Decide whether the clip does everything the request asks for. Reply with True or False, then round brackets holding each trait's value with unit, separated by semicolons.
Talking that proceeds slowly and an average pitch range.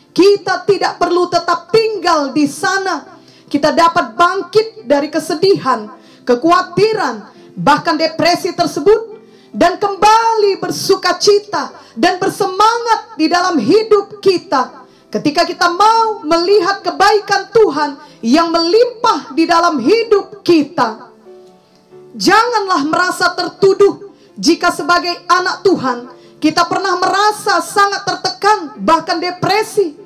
True (105 wpm; 3.3 semitones)